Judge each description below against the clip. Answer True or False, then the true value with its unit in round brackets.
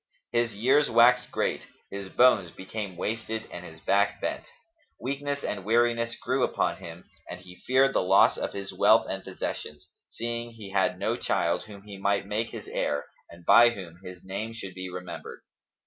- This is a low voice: True (100 Hz)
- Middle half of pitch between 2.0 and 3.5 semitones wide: False (4.2 semitones)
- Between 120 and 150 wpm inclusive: False (180 wpm)